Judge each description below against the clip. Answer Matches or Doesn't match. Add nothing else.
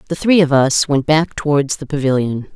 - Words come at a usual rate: Doesn't match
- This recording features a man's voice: Doesn't match